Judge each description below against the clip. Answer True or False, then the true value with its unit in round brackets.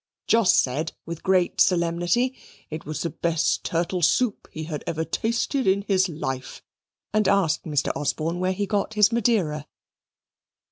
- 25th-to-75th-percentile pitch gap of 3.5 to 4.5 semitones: True (4.2 semitones)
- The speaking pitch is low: False (175 Hz)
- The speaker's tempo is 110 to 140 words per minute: False (150 wpm)